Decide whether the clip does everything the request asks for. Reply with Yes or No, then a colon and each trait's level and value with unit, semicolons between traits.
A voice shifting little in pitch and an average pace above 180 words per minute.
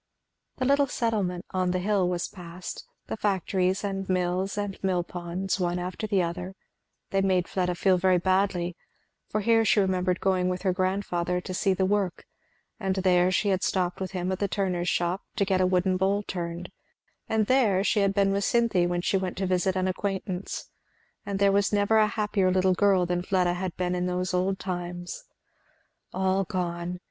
Yes: narrow, 1.6 semitones; average, 190 wpm